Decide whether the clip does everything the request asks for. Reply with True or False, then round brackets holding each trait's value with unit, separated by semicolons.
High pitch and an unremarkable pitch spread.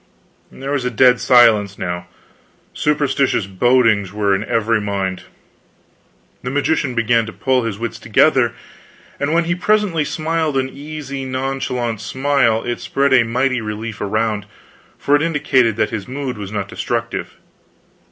False (125 Hz; 4.4 semitones)